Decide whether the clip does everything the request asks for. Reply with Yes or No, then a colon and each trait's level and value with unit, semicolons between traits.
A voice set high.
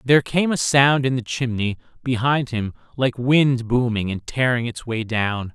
No: low, 125 Hz